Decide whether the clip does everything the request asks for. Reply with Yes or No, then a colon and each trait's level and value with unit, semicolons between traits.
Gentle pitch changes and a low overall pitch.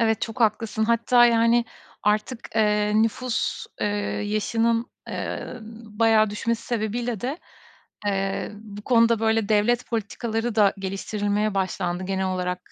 No: narrow, 2.1 semitones; high, 220 Hz